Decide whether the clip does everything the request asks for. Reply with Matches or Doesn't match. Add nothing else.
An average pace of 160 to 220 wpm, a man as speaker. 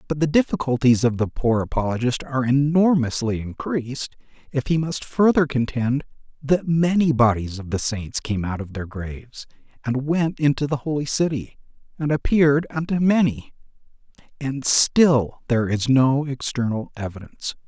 Doesn't match